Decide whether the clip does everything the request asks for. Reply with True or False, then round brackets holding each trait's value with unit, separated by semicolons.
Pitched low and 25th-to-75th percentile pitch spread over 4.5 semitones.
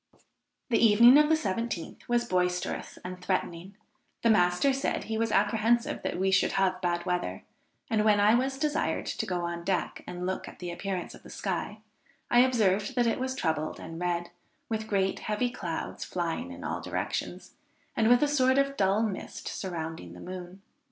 False (195 Hz; 5.0 semitones)